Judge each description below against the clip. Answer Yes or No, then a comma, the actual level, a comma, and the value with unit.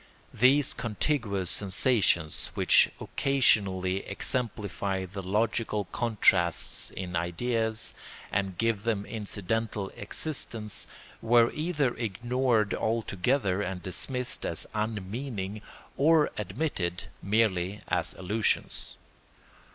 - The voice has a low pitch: Yes, low, 105 Hz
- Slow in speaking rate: Yes, slow, 90 wpm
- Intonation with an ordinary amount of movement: Yes, average, 3.8 semitones